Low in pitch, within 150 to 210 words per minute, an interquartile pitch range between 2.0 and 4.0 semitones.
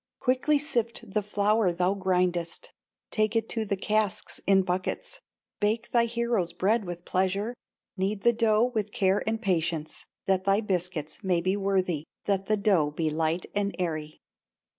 No: high, 195 Hz; average, 160 wpm; average, 3.3 semitones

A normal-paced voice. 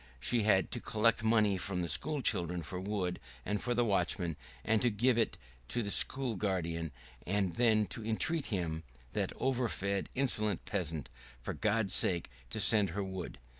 Yes: average, 170 wpm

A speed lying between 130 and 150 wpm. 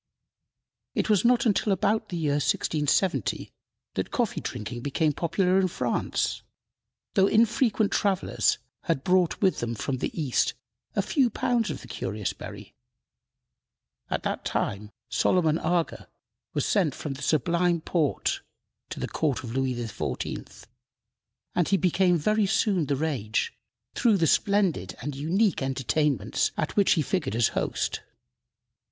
Yes: average, 140 wpm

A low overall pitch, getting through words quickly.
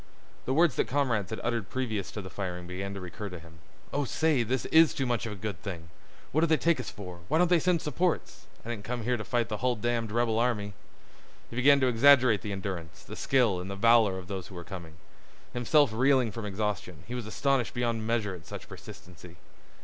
Yes: low, 115 Hz; fast, 225 wpm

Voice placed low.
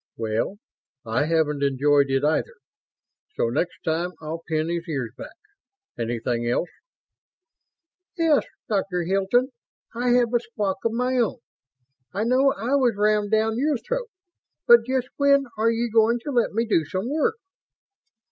No: high, 215 Hz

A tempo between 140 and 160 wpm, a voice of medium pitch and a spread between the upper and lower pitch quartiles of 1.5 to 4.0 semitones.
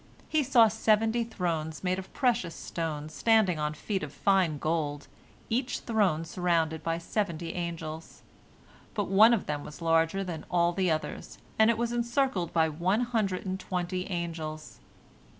No: average, 155 wpm; medium, 180 Hz; average, 5.0 semitones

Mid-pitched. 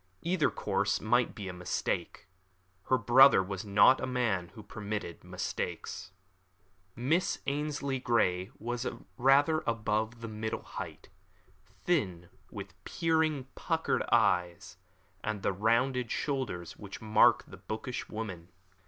No: low, 110 Hz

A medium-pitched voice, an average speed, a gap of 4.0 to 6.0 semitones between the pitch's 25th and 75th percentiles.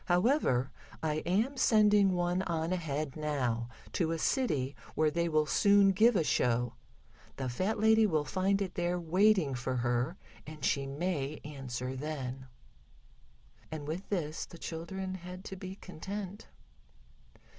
Yes: medium, 165 Hz; average, 145 wpm; wide, 5.4 semitones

